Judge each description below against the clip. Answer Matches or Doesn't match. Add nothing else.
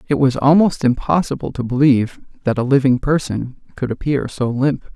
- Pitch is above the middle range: Doesn't match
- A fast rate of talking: Doesn't match